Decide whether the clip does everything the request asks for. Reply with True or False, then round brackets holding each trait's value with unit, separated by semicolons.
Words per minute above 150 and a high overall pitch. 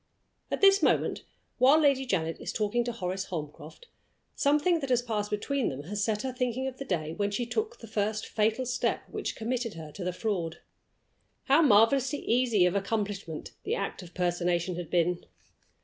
True (180 wpm; 215 Hz)